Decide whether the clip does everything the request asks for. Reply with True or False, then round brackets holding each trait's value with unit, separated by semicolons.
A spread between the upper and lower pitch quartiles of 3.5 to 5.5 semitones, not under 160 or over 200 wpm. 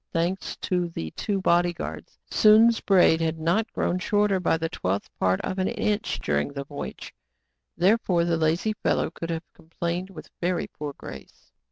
False (3.0 semitones; 175 wpm)